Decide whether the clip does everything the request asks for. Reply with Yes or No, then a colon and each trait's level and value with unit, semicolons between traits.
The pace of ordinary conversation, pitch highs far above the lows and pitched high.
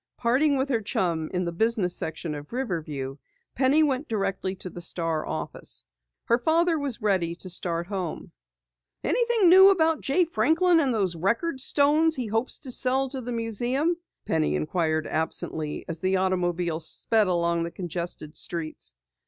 Yes: average, 160 wpm; wide, 8.1 semitones; high, 200 Hz